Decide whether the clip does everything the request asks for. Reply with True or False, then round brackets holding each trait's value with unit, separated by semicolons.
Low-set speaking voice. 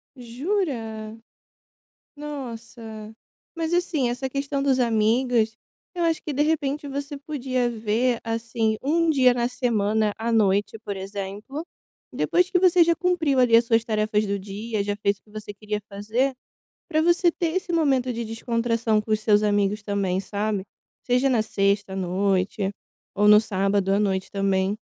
False (225 Hz)